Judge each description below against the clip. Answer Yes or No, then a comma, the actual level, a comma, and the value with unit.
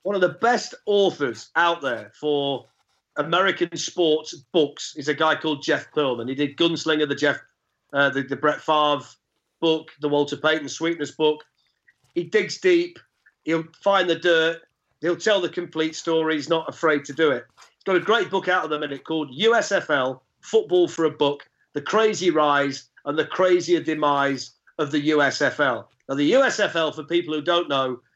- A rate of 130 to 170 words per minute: No, average, 180 wpm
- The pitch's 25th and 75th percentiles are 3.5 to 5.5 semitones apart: No, average, 3.1 semitones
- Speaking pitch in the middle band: Yes, medium, 155 Hz